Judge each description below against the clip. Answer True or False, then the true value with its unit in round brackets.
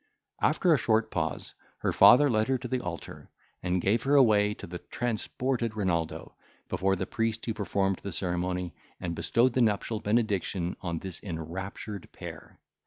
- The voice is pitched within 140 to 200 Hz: False (105 Hz)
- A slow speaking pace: False (165 wpm)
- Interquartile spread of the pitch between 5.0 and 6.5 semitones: False (4.3 semitones)